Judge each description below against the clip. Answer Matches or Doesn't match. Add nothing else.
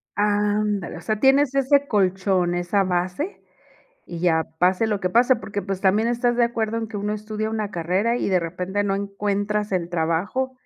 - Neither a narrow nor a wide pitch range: Matches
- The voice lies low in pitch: Doesn't match